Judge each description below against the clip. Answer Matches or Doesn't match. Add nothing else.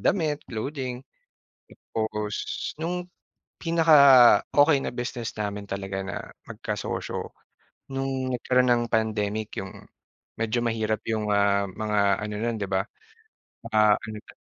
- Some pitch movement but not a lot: Matches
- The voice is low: Matches